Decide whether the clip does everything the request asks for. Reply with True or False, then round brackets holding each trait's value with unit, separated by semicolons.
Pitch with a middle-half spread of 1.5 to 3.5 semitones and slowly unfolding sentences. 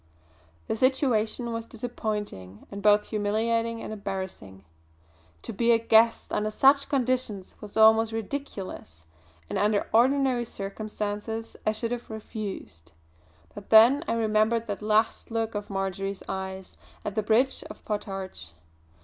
True (2.5 semitones; 130 wpm)